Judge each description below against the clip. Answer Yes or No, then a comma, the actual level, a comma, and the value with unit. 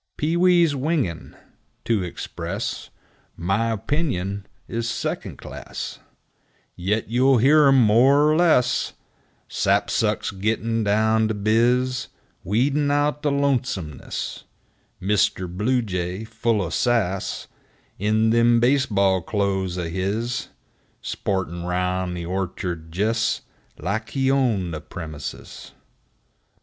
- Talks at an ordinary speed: No, slow, 110 wpm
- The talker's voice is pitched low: Yes, low, 110 Hz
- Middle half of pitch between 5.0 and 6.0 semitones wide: Yes, wide, 5.5 semitones